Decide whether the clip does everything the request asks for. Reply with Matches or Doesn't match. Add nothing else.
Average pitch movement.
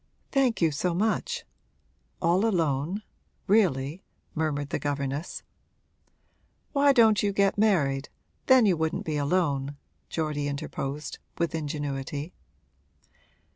Doesn't match